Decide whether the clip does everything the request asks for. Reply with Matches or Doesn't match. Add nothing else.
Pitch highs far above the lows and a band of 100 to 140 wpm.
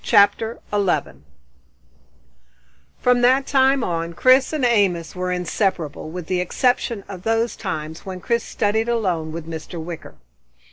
Matches